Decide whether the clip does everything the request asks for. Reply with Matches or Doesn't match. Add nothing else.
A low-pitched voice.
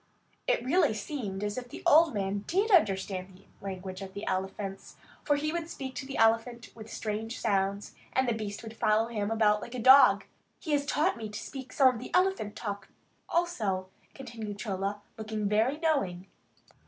Doesn't match